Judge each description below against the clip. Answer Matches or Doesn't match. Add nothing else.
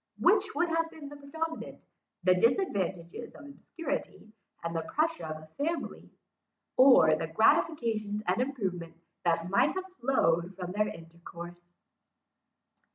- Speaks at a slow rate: Matches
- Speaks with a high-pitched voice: Matches